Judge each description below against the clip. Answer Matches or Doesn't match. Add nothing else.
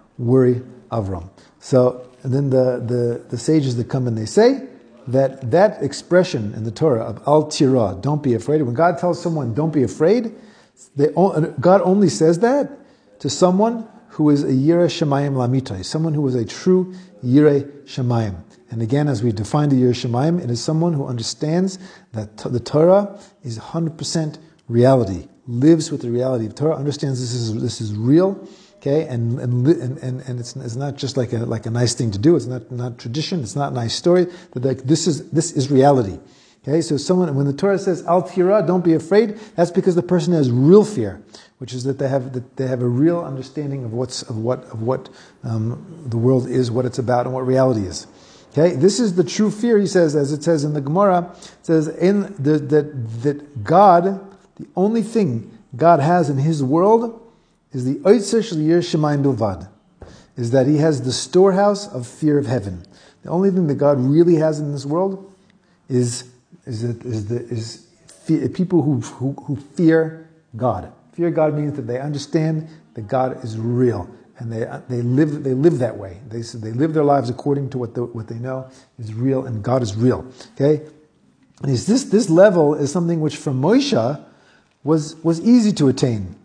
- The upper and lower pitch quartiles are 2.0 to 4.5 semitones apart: Doesn't match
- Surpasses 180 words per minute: Matches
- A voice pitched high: Doesn't match